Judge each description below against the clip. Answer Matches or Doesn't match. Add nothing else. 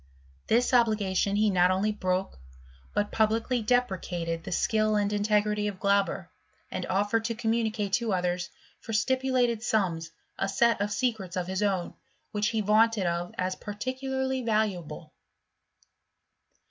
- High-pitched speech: Matches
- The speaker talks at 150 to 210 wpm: Doesn't match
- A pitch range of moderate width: Matches